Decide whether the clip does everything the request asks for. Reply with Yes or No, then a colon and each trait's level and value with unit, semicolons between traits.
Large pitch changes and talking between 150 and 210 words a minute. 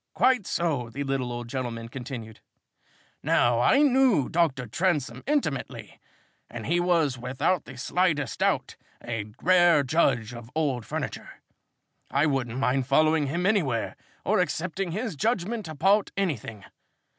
No: wide, 6.4 semitones; slow, 135 wpm